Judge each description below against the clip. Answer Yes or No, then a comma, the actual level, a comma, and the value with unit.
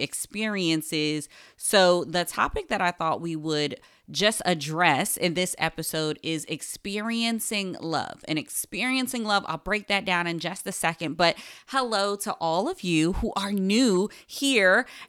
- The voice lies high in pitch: No, medium, 180 Hz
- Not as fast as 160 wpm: Yes, average, 150 wpm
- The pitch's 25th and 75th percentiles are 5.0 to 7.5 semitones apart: No, average, 4.4 semitones